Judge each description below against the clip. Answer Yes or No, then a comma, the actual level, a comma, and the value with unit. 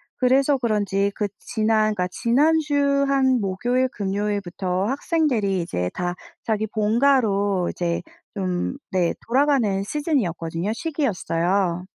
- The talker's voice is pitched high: Yes, high, 210 Hz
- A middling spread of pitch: No, wide, 5.8 semitones